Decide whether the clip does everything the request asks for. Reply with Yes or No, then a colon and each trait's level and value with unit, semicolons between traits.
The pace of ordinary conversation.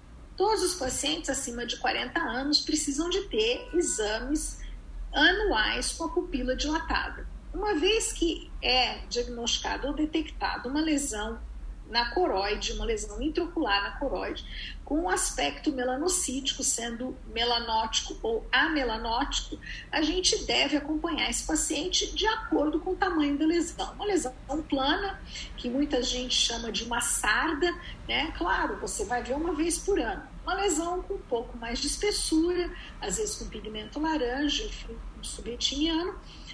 Yes: average, 145 wpm